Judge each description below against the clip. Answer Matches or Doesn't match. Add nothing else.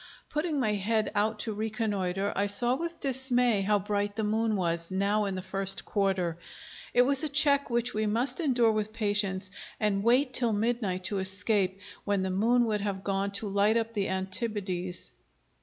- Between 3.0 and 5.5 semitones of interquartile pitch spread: Matches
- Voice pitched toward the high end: Matches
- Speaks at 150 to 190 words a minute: Matches